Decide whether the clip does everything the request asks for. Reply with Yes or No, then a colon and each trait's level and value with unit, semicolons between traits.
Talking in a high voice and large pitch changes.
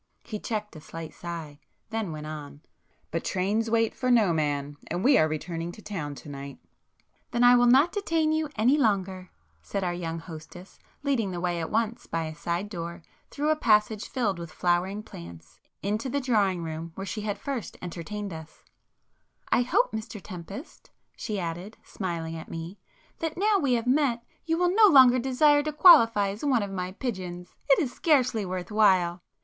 Yes: high, 200 Hz; wide, 6.3 semitones